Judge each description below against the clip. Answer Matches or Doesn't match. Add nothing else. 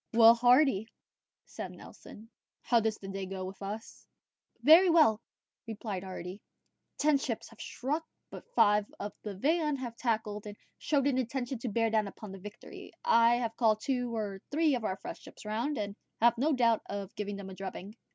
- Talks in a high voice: Matches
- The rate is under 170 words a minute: Doesn't match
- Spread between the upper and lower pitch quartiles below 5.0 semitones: Matches